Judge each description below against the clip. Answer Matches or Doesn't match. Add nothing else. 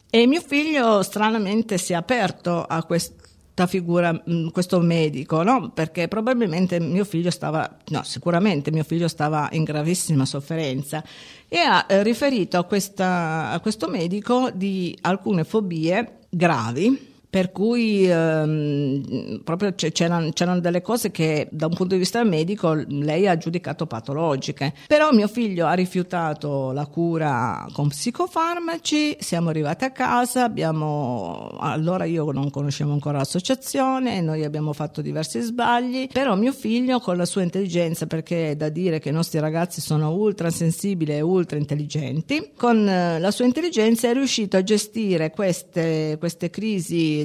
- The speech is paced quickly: Doesn't match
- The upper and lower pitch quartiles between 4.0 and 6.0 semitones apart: Matches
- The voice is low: Doesn't match